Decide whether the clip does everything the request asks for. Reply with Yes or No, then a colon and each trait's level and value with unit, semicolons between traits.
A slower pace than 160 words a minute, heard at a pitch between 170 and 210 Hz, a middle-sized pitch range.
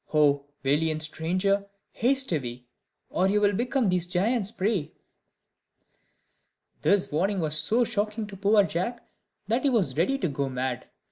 No: average, 140 wpm; high, 190 Hz; wide, 5.7 semitones